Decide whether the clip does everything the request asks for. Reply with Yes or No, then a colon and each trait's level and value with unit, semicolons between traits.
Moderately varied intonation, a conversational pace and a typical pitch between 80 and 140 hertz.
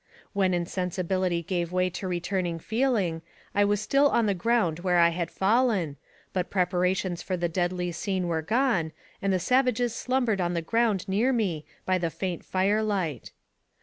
No: average, 3.6 semitones; average, 175 wpm; medium, 185 Hz